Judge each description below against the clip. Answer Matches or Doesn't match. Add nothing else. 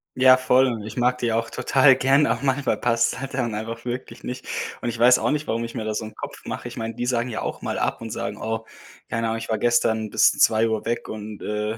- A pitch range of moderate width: Doesn't match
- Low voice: Matches